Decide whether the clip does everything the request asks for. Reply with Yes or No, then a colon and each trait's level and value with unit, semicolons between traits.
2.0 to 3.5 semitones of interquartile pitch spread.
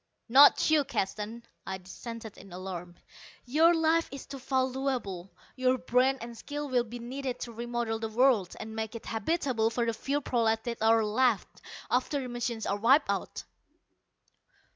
Yes: average, 3.0 semitones